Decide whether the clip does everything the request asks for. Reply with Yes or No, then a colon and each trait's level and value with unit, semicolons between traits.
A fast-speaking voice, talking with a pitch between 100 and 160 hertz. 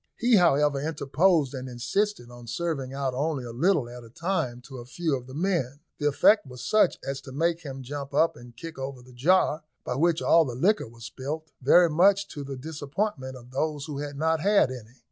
Yes: fast, 215 wpm; medium, 140 Hz